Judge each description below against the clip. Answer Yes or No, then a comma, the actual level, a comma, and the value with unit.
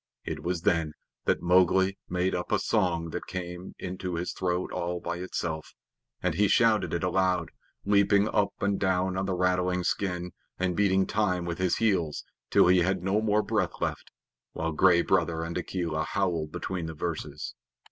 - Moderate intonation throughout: No, narrow, 1.8 semitones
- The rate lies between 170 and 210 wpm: Yes, average, 175 wpm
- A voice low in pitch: Yes, very low, 90 Hz